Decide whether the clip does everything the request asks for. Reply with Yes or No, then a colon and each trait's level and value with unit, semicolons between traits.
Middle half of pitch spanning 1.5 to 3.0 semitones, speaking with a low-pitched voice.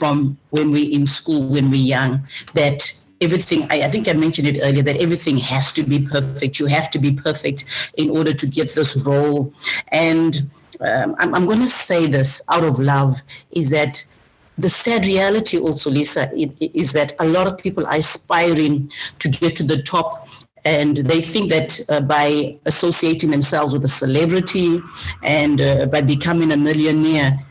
No: narrow, 2.4 semitones; medium, 150 Hz